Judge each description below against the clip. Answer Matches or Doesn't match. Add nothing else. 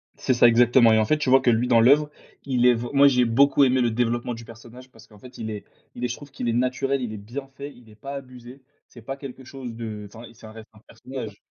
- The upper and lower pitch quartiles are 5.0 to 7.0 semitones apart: Doesn't match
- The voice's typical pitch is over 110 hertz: Matches